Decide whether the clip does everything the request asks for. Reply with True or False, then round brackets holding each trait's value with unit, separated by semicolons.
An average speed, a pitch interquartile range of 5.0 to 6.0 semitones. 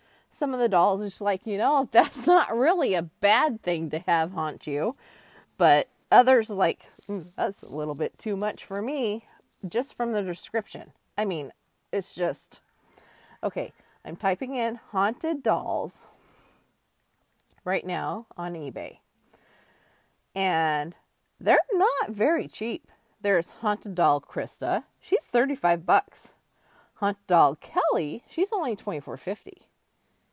False (130 wpm; 5.6 semitones)